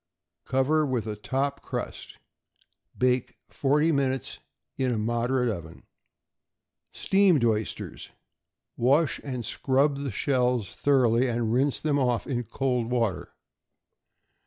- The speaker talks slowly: Yes, slow, 110 wpm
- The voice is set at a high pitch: No, low, 130 Hz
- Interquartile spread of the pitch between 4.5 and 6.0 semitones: No, average, 2.9 semitones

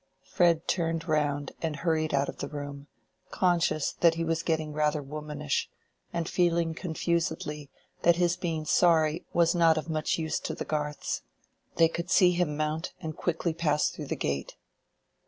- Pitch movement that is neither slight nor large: No, narrow, 2.0 semitones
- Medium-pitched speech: Yes, medium, 160 Hz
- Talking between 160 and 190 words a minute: Yes, average, 165 wpm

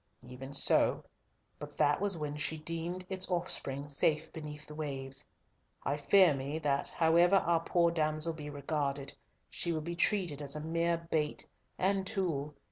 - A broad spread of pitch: No, average, 2.8 semitones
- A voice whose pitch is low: No, medium, 155 Hz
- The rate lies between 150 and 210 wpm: Yes, average, 160 wpm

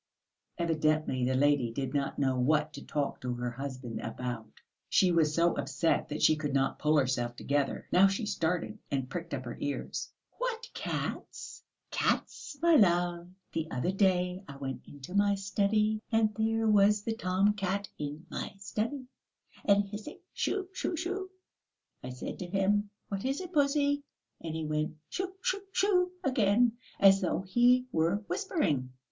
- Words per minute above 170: No, average, 165 wpm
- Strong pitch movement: Yes, wide, 7.0 semitones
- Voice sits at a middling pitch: Yes, medium, 180 Hz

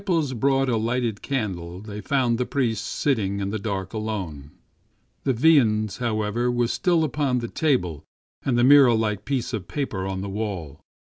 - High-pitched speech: No, low, 115 Hz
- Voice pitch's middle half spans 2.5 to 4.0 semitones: No, average, 4.7 semitones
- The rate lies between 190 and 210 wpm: Yes, average, 195 wpm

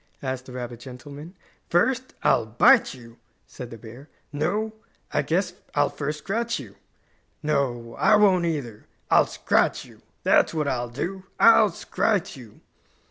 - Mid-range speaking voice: Yes, medium, 145 Hz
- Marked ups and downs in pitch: Yes, wide, 7.4 semitones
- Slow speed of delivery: No, average, 145 wpm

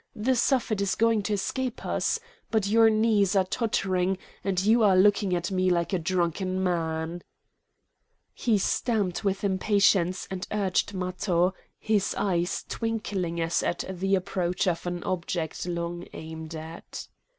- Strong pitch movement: No, average, 3.0 semitones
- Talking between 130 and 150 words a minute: Yes, average, 145 wpm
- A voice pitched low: No, high, 190 Hz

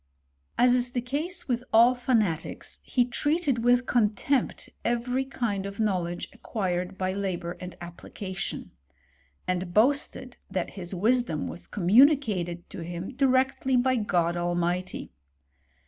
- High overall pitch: Yes, high, 215 Hz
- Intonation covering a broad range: Yes, wide, 5.9 semitones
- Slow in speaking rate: Yes, slow, 130 wpm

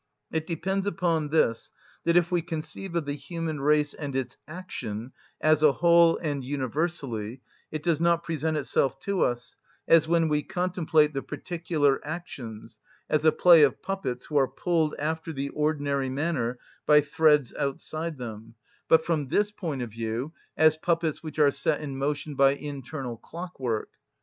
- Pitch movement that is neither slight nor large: Yes, average, 3.4 semitones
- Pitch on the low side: No, medium, 150 Hz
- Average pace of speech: Yes, average, 165 wpm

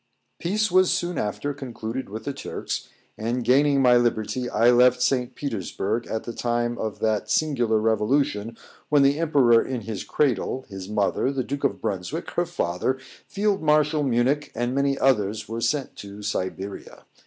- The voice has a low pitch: Yes, low, 125 Hz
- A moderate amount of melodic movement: Yes, average, 4.3 semitones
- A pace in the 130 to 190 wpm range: Yes, average, 165 wpm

